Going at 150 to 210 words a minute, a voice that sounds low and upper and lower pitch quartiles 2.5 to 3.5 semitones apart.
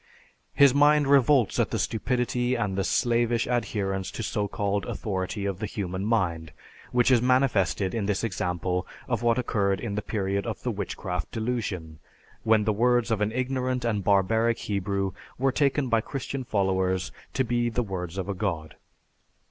No: average, 170 wpm; low, 110 Hz; average, 4.0 semitones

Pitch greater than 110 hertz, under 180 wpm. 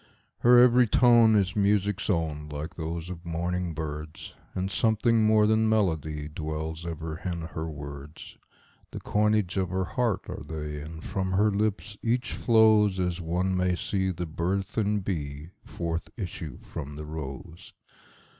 No: very low, 90 Hz; average, 140 wpm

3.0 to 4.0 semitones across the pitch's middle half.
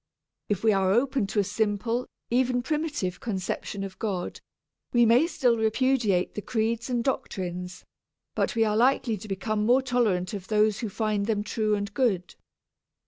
Yes: average, 3.4 semitones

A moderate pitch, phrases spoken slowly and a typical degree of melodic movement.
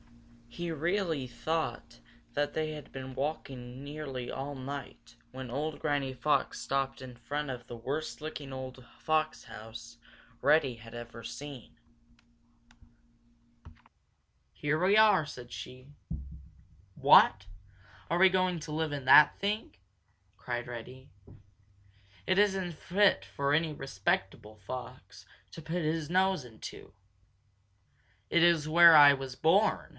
Yes: medium, 145 Hz; slow, 125 wpm; average, 4.1 semitones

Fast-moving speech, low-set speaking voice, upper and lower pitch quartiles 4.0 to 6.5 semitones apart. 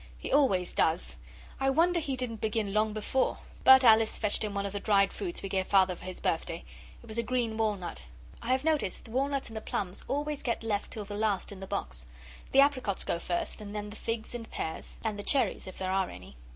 No: fast, 230 wpm; high, 215 Hz; average, 4.7 semitones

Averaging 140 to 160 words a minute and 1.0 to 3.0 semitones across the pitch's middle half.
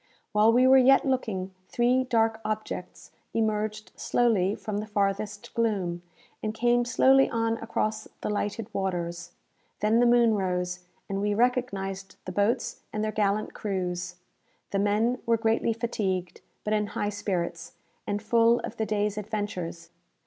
Yes: average, 150 wpm; average, 2.7 semitones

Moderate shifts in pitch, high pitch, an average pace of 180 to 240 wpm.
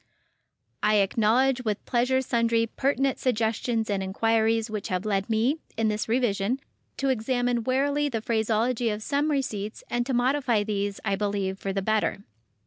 No: average, 3.2 semitones; high, 225 Hz; average, 155 wpm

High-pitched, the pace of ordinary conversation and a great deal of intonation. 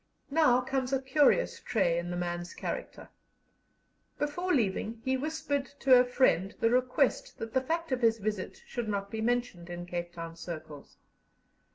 Yes: high, 240 Hz; average, 165 wpm; wide, 7.1 semitones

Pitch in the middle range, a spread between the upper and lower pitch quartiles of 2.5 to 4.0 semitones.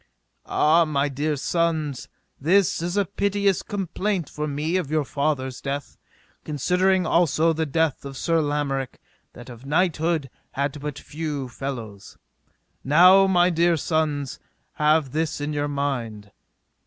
Yes: medium, 150 Hz; average, 3.4 semitones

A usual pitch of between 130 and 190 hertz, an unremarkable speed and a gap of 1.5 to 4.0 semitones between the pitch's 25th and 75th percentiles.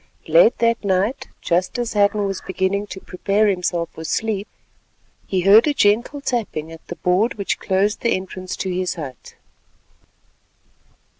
No: high, 200 Hz; average, 150 wpm; average, 3.1 semitones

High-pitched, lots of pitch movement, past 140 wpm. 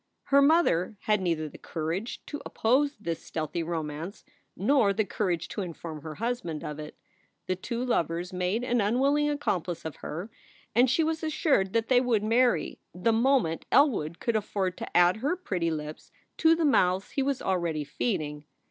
Yes: high, 200 Hz; wide, 6.9 semitones; average, 175 wpm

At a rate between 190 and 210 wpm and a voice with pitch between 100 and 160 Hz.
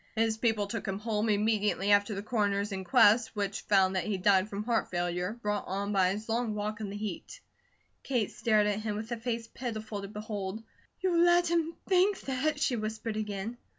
No: average, 195 wpm; high, 215 Hz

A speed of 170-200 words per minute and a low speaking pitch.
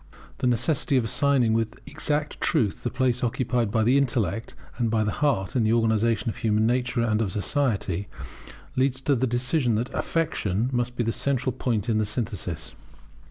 Yes: average, 180 wpm; low, 120 Hz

